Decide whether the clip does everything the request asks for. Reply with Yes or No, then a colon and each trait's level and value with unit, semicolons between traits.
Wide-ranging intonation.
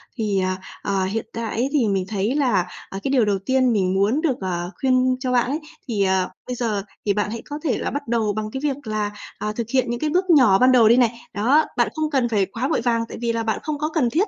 No: average, 4.3 semitones